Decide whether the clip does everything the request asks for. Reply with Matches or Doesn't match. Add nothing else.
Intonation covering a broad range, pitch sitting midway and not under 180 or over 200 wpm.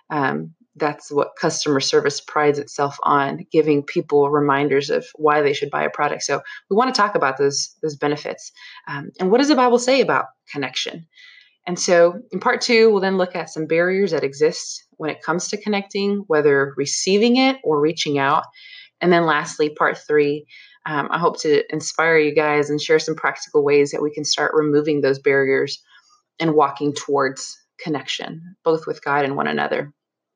Matches